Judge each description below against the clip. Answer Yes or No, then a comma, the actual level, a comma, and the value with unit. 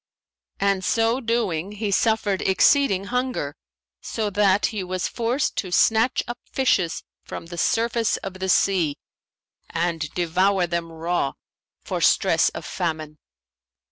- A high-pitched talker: Yes, high, 195 Hz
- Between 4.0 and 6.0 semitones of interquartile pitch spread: Yes, average, 4.6 semitones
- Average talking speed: No, slow, 130 wpm